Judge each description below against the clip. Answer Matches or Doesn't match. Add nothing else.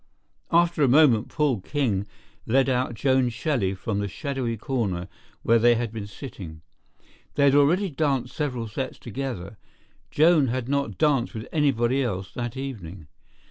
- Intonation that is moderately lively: Matches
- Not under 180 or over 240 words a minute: Doesn't match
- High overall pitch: Doesn't match